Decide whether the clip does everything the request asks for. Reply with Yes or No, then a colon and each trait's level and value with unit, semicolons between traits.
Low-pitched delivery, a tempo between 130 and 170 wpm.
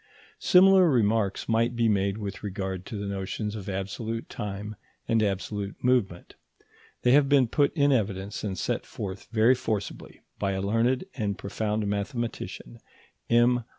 Yes: low, 105 Hz; average, 150 wpm